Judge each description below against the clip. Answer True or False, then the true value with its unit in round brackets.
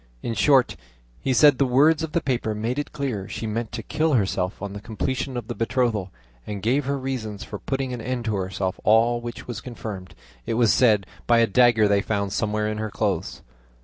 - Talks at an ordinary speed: False (215 wpm)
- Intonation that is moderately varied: True (3.5 semitones)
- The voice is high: False (115 Hz)